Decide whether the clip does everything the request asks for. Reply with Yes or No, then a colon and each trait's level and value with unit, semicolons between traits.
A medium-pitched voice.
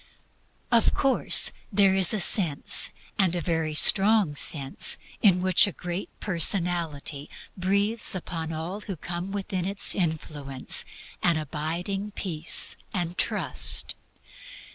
Yes: medium, 180 Hz